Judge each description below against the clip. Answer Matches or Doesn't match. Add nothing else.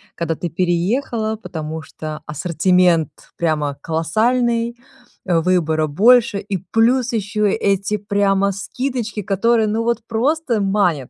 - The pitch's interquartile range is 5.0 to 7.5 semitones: Matches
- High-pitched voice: Matches